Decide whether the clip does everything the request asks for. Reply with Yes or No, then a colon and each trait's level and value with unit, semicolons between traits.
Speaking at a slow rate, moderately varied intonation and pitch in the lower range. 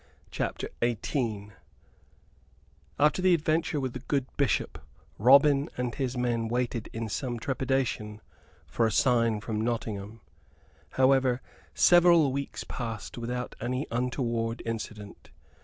Yes: slow, 115 wpm; average, 3.0 semitones; low, 125 Hz